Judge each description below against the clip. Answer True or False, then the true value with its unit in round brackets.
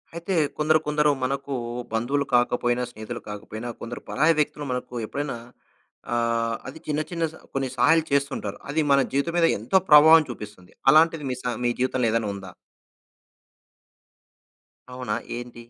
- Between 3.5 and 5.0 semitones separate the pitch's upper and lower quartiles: True (4.1 semitones)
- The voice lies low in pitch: True (130 Hz)